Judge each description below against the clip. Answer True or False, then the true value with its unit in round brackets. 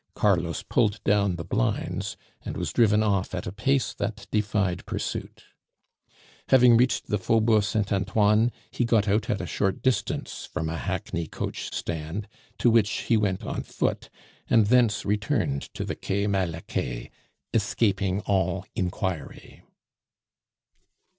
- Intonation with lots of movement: False (2.9 semitones)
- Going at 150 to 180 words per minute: False (140 wpm)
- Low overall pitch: True (100 Hz)